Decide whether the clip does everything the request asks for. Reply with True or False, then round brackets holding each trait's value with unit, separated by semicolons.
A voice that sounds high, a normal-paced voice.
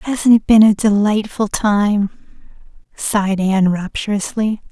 False (205 Hz; 115 wpm)